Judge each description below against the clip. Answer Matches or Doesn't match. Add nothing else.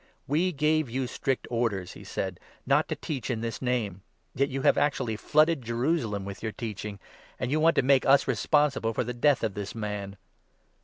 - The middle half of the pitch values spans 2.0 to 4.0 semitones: Doesn't match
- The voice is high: Doesn't match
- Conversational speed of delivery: Doesn't match